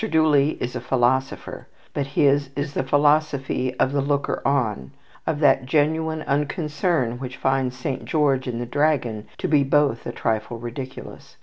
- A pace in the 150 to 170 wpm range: Yes, average, 160 wpm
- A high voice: No, medium, 140 Hz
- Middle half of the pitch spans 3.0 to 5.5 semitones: No, narrow, 2.6 semitones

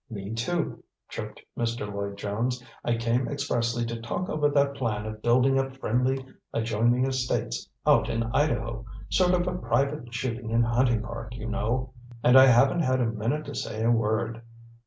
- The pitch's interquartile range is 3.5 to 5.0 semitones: No, narrow, 2.6 semitones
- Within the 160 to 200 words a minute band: Yes, average, 170 wpm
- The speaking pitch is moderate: No, low, 120 Hz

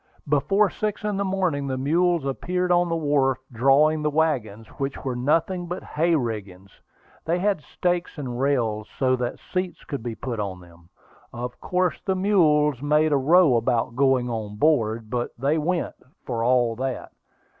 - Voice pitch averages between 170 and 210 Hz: No, medium, 140 Hz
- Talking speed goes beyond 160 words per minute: Yes, average, 170 wpm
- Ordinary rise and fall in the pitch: No, wide, 6.1 semitones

